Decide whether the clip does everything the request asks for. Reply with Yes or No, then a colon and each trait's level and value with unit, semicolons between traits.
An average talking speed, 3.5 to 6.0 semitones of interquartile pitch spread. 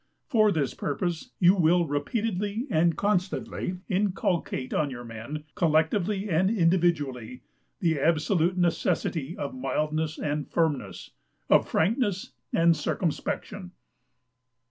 No: slow, 105 wpm; average, 3.8 semitones